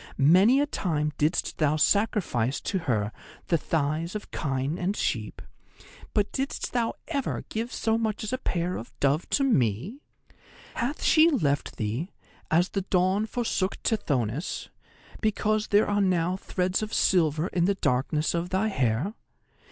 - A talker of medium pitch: Yes, medium, 180 Hz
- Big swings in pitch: Yes, wide, 6.4 semitones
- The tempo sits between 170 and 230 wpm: No, average, 150 wpm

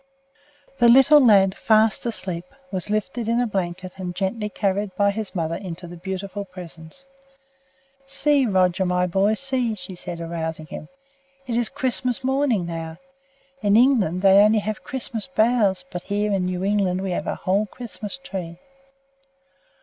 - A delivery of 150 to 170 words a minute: Yes, average, 155 wpm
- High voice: Yes, high, 200 Hz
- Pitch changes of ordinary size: Yes, average, 4.2 semitones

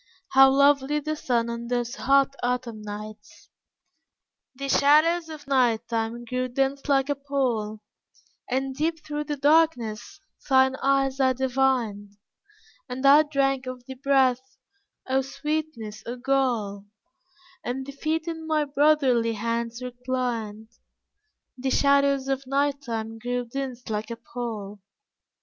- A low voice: No, very high, 260 Hz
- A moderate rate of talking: No, slow, 130 wpm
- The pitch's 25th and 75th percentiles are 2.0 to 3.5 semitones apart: Yes, average, 3.0 semitones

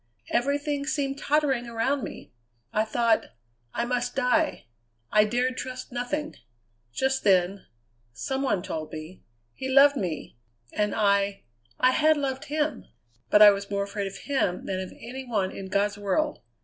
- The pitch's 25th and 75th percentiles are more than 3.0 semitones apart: Yes, wide, 5.5 semitones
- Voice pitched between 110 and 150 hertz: No, high, 240 Hz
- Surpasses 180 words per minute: No, average, 155 wpm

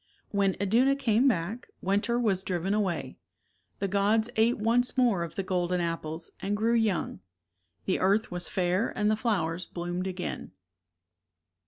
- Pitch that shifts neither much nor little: Yes, average, 3.8 semitones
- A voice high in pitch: Yes, high, 200 Hz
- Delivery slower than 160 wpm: Yes, average, 150 wpm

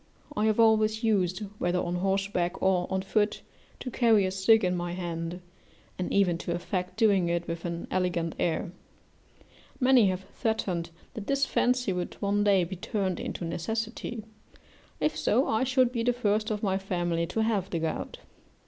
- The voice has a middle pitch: No, high, 195 Hz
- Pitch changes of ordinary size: Yes, average, 3.9 semitones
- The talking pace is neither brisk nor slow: Yes, average, 175 wpm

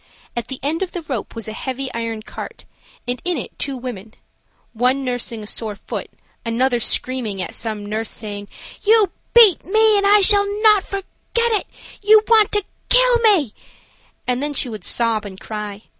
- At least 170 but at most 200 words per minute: Yes, average, 175 wpm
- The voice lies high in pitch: Yes, very high, 255 Hz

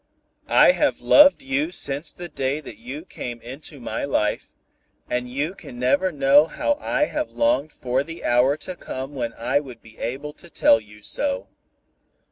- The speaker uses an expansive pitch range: Yes, wide, 6.2 semitones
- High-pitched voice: No, medium, 140 Hz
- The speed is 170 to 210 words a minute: Yes, average, 175 wpm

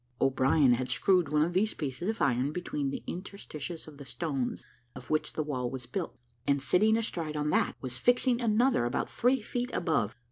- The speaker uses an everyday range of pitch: No, wide, 7.0 semitones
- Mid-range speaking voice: Yes, medium, 150 Hz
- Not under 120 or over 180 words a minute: No, average, 190 wpm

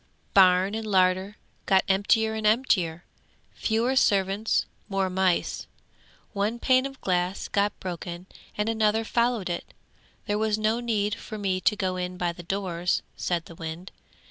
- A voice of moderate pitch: No, high, 195 Hz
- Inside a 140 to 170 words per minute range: Yes, average, 150 wpm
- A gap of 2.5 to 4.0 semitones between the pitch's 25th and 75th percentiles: Yes, average, 3.1 semitones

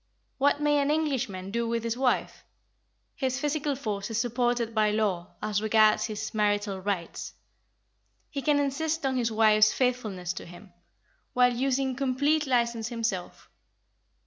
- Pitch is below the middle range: No, high, 235 Hz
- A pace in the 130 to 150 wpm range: Yes, average, 145 wpm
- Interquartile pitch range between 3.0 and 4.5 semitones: Yes, average, 4.2 semitones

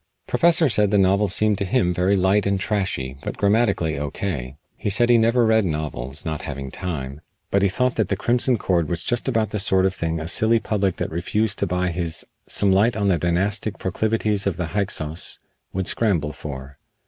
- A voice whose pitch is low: Yes, very low, 95 Hz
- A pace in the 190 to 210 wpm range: Yes, average, 200 wpm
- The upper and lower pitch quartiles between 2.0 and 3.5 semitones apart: No, average, 4.5 semitones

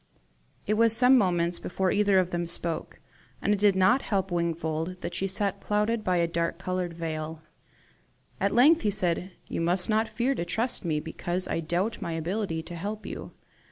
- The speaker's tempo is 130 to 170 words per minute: No, average, 190 wpm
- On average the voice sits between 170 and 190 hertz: Yes, medium, 185 Hz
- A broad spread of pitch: No, average, 3.7 semitones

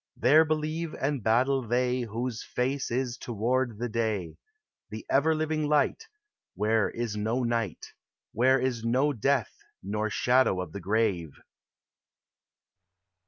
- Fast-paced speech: No, average, 140 wpm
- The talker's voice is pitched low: Yes, low, 120 Hz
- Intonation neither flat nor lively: Yes, average, 3.5 semitones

